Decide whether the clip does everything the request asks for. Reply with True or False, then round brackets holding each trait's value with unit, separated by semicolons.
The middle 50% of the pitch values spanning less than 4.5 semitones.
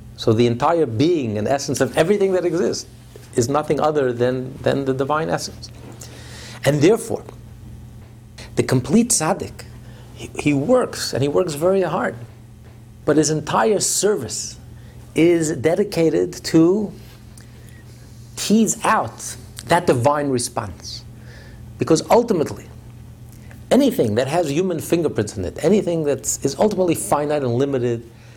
False (5.6 semitones)